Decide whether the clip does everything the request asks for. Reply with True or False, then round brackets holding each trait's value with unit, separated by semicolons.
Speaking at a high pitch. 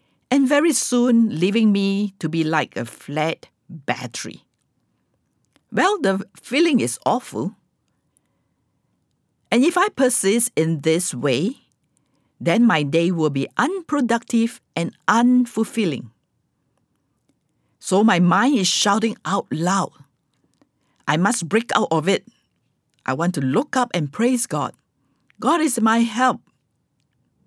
True (200 Hz)